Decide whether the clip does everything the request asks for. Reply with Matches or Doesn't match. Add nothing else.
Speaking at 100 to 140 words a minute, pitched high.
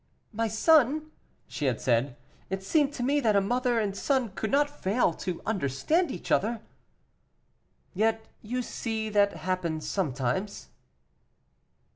Matches